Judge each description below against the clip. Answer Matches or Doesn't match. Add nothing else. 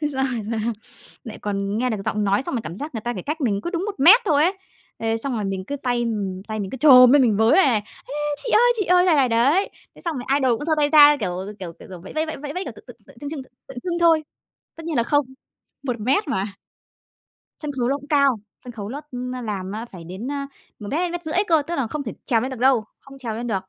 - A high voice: Matches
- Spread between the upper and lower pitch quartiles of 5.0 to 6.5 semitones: Matches